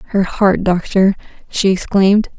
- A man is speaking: No, female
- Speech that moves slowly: Yes, slow, 125 wpm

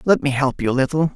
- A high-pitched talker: No, medium, 140 Hz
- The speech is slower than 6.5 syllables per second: No, 6.7 syllables/s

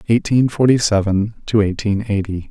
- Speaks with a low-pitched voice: Yes, low, 105 Hz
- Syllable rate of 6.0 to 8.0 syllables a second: No, 5.0 syllables/s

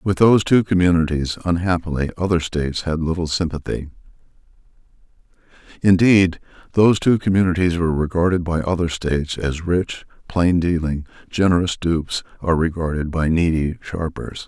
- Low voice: Yes, very low, 85 Hz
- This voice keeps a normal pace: No, slow, 120 wpm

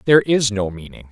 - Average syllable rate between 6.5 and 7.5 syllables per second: No, 6.2 syllables/s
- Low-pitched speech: Yes, low, 115 Hz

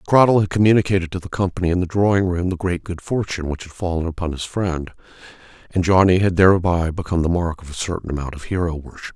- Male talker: Yes, male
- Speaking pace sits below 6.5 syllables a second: No, 6.7 syllables/s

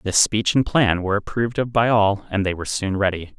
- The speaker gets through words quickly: Yes, fast, 250 wpm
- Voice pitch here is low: Yes, low, 105 Hz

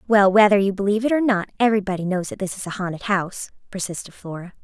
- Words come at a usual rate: No, fast, 220 wpm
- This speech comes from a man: No, female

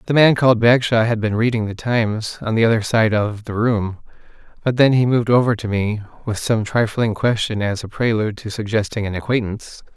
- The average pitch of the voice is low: Yes, low, 110 Hz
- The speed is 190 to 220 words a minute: Yes, fast, 205 wpm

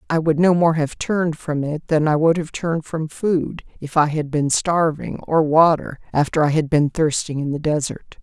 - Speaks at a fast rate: Yes, fast, 220 wpm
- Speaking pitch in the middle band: Yes, medium, 155 Hz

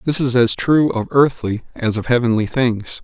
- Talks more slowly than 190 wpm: No, average, 200 wpm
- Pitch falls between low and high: No, low, 120 Hz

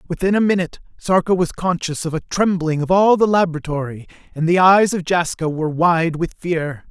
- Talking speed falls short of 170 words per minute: No, average, 190 wpm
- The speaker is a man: Yes, male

